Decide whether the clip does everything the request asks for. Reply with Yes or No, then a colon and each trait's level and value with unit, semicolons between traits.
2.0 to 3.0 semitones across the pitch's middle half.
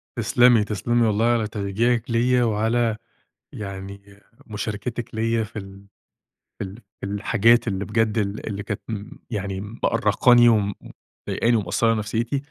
Yes: narrow, 2.5 semitones